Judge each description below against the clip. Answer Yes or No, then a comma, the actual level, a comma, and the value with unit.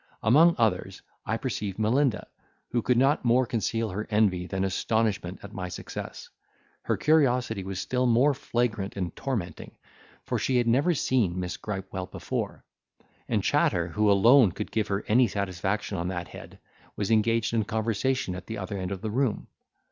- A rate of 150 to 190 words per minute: Yes, average, 170 wpm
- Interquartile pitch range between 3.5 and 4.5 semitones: Yes, average, 4.2 semitones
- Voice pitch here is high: No, low, 110 Hz